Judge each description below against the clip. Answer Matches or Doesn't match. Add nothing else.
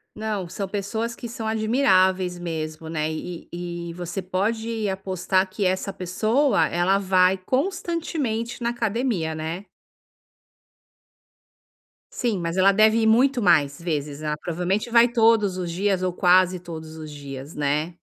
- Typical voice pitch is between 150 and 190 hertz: Matches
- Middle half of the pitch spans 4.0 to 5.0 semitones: Matches